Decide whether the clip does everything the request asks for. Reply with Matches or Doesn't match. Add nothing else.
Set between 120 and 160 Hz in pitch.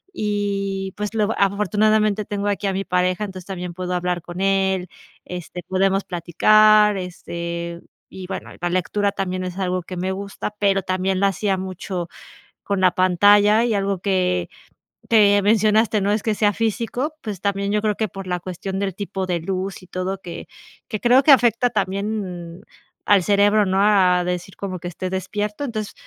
Doesn't match